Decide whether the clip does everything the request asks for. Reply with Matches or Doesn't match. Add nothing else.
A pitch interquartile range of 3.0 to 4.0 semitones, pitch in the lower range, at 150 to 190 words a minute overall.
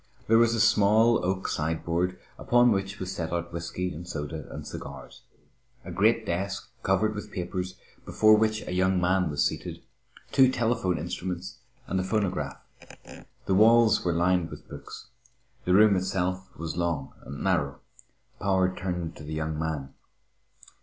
Matches